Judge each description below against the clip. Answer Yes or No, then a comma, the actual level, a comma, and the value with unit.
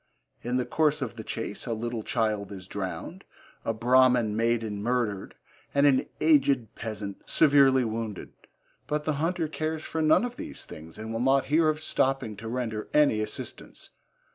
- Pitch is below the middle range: Yes, low, 120 Hz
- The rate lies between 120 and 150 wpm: No, average, 165 wpm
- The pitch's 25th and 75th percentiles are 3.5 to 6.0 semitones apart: Yes, average, 4.9 semitones